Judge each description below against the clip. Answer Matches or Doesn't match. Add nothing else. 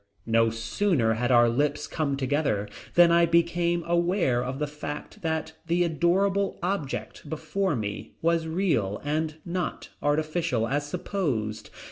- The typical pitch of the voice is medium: Matches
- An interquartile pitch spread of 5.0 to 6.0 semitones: Matches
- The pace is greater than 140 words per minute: Doesn't match